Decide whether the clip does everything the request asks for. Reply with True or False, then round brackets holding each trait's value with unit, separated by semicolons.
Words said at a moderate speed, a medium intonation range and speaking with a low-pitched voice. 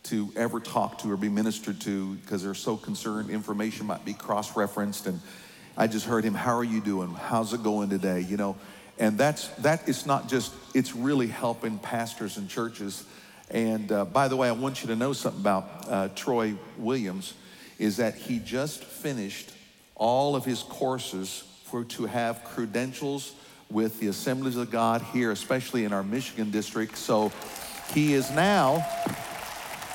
True (175 wpm; 3.7 semitones; 115 Hz)